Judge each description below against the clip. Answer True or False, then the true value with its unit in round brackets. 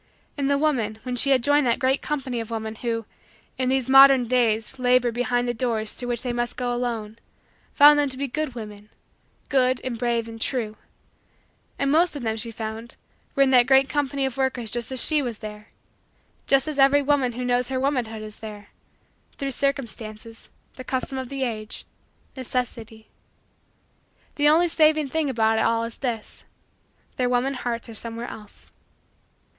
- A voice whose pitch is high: True (245 Hz)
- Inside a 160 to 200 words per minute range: True (180 wpm)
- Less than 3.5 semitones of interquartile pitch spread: True (3.0 semitones)